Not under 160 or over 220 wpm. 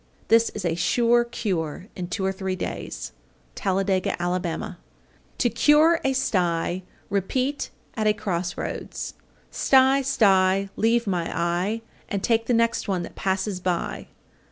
No: average, 145 wpm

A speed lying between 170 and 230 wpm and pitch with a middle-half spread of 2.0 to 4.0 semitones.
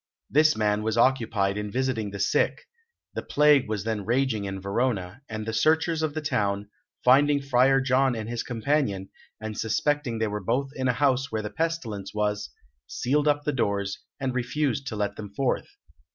No: average, 180 wpm; average, 4.7 semitones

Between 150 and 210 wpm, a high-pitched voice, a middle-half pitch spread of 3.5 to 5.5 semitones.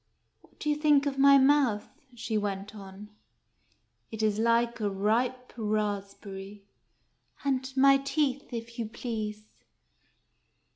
No: average, 140 wpm; high, 230 Hz; average, 4.2 semitones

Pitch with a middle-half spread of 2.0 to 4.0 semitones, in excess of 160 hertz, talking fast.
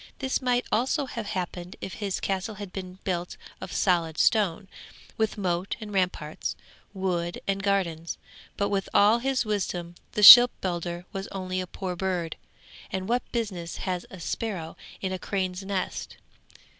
No: narrow, 2.6 semitones; high, 190 Hz; average, 155 wpm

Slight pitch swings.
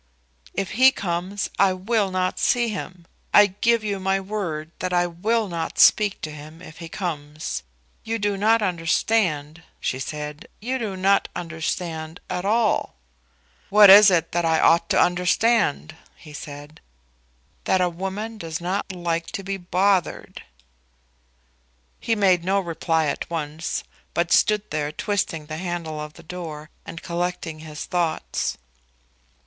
No: average, 3.7 semitones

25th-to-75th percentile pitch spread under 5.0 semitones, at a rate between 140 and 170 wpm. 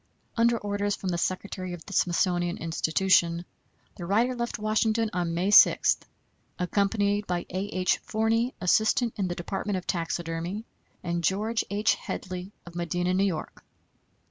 Yes: average, 3.2 semitones; average, 145 wpm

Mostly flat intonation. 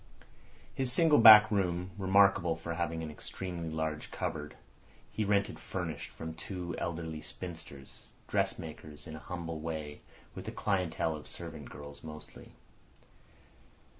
No: average, 3.2 semitones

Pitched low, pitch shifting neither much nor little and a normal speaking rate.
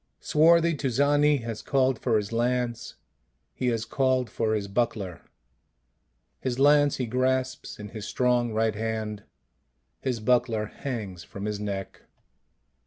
No: low, 120 Hz; average, 3.3 semitones; slow, 130 wpm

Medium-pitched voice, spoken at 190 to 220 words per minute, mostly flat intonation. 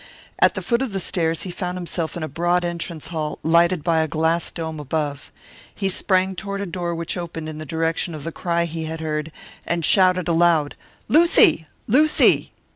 Yes: medium, 170 Hz; average, 195 wpm; narrow, 2.1 semitones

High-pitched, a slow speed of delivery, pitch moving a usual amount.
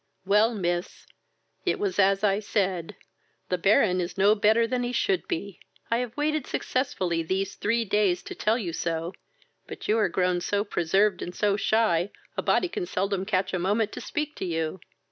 No: high, 200 Hz; average, 185 wpm; average, 3.5 semitones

